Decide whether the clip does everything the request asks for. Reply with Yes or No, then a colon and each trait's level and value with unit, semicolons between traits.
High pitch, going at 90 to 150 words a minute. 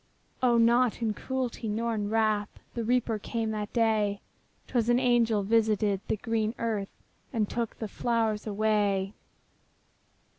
Yes: high, 220 Hz; average, 140 wpm